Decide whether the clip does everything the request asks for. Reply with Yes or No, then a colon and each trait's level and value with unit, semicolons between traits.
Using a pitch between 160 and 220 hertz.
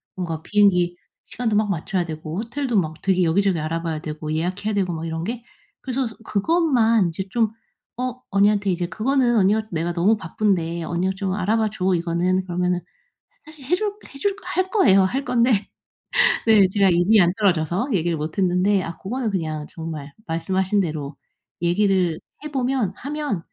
Yes: high, 190 Hz